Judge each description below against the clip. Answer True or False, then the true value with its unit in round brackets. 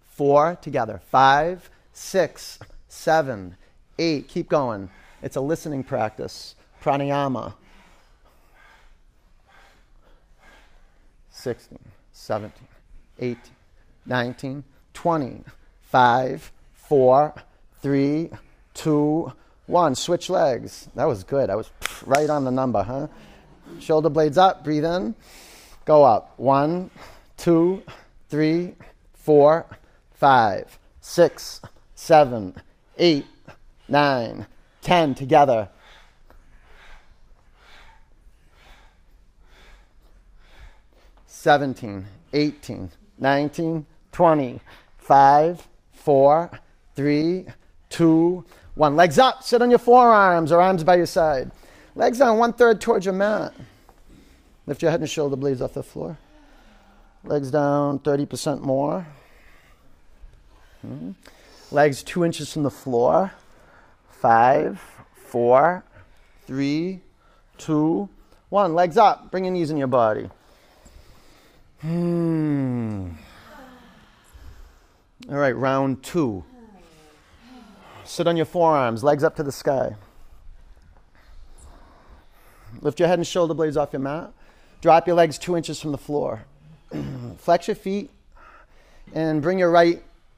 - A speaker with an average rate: False (100 wpm)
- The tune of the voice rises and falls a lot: True (5.8 semitones)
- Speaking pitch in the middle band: True (145 Hz)